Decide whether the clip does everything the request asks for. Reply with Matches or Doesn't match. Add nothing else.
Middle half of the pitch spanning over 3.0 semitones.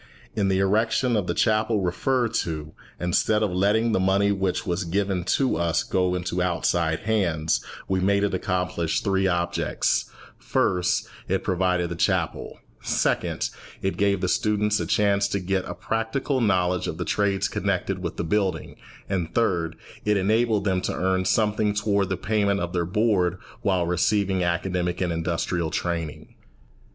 Doesn't match